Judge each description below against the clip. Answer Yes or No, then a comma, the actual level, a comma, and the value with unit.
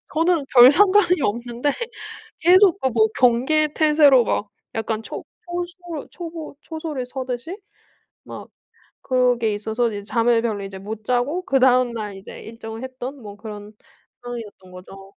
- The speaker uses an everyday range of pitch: No, wide, 5.8 semitones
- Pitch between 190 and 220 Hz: No, high, 245 Hz